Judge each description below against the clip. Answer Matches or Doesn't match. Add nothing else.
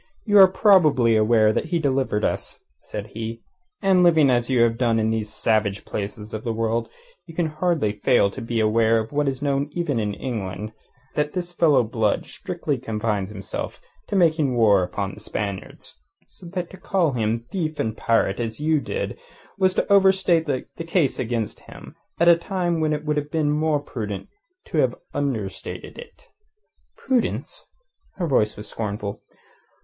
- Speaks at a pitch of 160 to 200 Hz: Doesn't match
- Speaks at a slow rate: Doesn't match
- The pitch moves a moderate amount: Doesn't match